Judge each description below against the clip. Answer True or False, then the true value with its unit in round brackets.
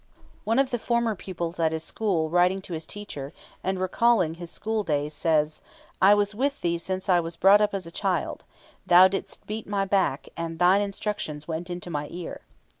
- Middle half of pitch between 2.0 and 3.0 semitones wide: False (3.8 semitones)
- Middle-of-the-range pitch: True (180 Hz)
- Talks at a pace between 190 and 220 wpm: True (195 wpm)